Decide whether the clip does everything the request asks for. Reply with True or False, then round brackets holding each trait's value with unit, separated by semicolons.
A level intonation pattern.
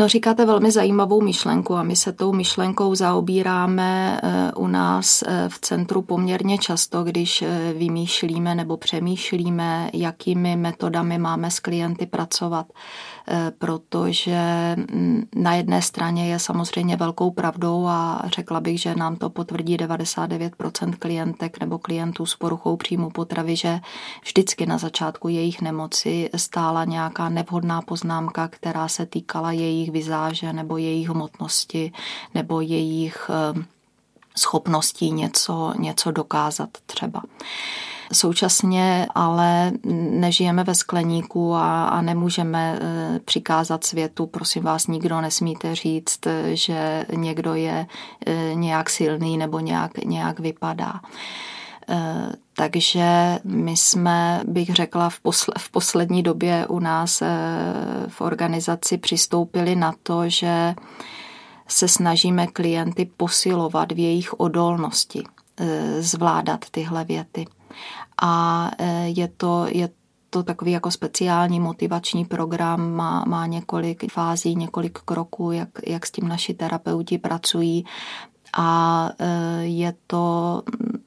True (1.2 semitones)